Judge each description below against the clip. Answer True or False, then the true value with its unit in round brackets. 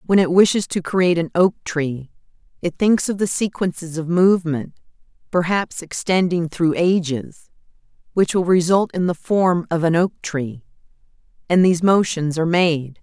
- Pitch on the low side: False (170 Hz)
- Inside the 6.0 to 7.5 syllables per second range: False (4.8 syllables/s)